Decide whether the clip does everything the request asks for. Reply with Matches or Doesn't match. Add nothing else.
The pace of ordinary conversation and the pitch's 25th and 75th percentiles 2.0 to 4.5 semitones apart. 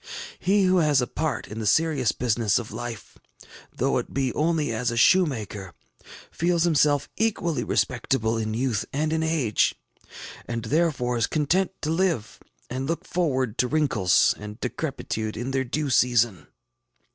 Doesn't match